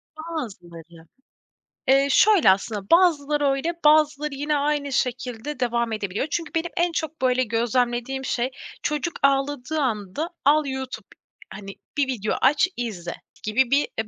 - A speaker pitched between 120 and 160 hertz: No, very high, 265 Hz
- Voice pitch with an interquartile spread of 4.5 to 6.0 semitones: Yes, average, 4.8 semitones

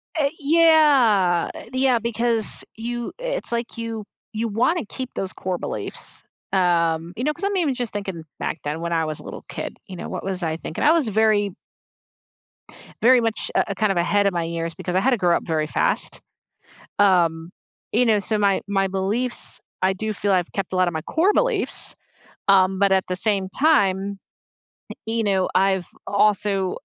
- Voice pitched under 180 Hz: No, high, 200 Hz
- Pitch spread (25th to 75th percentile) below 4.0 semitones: No, average, 4.4 semitones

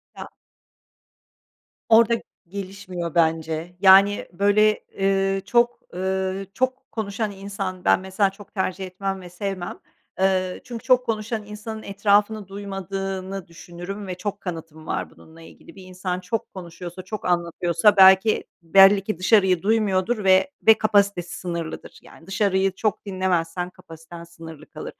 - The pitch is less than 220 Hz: Yes, high, 190 Hz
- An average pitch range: No, narrow, 2.3 semitones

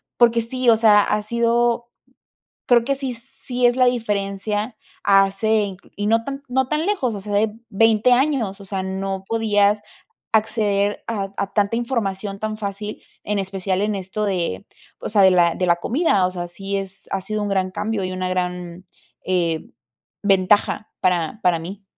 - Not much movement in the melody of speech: No, average, 3.1 semitones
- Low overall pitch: No, high, 205 Hz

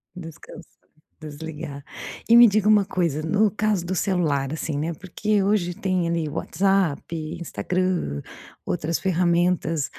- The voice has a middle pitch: Yes, medium, 175 Hz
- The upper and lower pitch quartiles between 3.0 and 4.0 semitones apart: Yes, average, 3.5 semitones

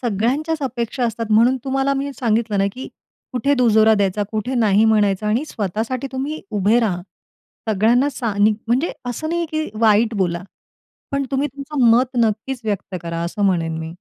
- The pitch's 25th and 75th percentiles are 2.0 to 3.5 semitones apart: No, average, 4.2 semitones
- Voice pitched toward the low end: No, high, 230 Hz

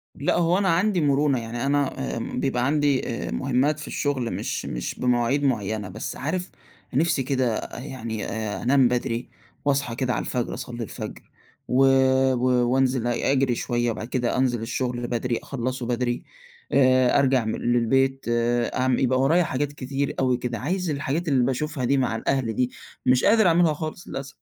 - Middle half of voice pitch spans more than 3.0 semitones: No, narrow, 2.6 semitones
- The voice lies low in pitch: Yes, low, 130 Hz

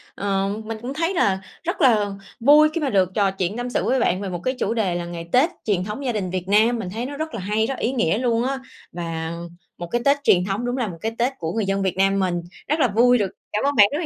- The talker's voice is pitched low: No, high, 215 Hz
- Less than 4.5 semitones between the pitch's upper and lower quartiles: No, average, 5.1 semitones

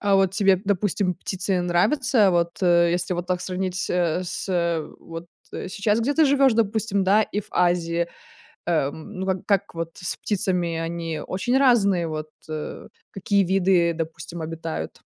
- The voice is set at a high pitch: No, medium, 180 Hz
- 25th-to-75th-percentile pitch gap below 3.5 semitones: Yes, average, 2.9 semitones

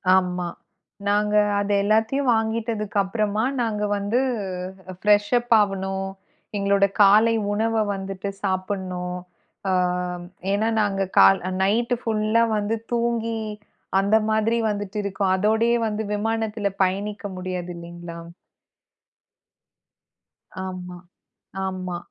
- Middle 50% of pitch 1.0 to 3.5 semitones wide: Yes, narrow, 2.6 semitones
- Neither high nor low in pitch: No, high, 205 Hz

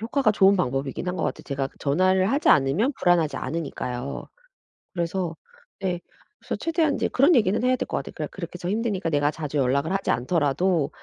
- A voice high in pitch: No, medium, 175 Hz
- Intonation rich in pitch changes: Yes, wide, 5.7 semitones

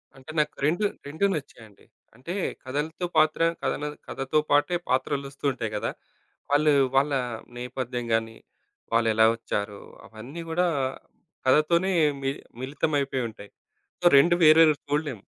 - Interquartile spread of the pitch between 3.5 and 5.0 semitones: Yes, average, 4.2 semitones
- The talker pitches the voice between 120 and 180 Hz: Yes, medium, 140 Hz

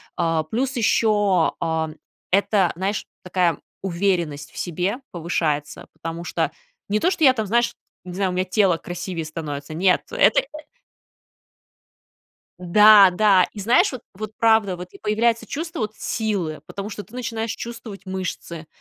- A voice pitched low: No, high, 195 Hz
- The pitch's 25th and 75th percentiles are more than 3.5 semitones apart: Yes, average, 4.1 semitones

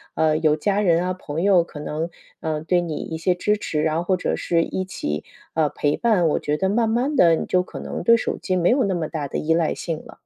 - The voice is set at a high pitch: No, medium, 170 Hz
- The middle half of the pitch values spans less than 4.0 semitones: Yes, average, 3.3 semitones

